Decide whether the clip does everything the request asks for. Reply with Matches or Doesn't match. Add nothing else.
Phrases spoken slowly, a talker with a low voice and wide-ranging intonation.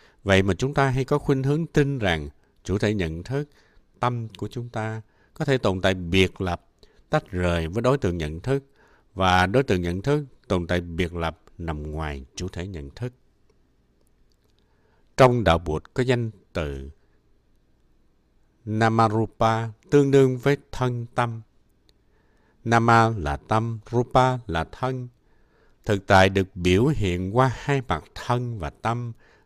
Matches